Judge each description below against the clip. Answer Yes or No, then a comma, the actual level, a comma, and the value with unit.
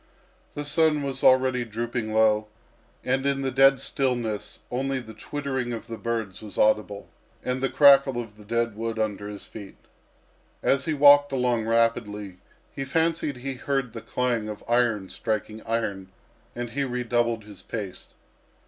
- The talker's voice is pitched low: Yes, low, 120 Hz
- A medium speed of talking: Yes, average, 155 wpm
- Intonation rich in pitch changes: No, average, 3.7 semitones